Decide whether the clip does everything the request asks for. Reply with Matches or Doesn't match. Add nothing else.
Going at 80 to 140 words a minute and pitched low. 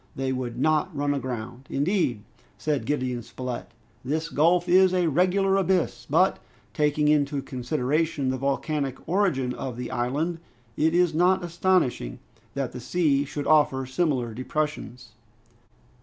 Doesn't match